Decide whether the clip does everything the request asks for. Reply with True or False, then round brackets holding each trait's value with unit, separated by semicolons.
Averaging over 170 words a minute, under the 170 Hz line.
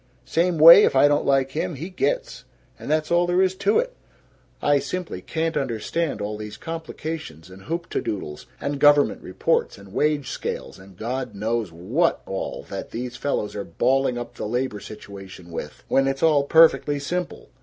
True (180 wpm; 140 Hz)